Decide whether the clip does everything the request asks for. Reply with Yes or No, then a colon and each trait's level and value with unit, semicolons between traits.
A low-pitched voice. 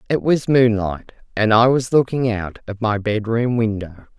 Yes: low, 115 Hz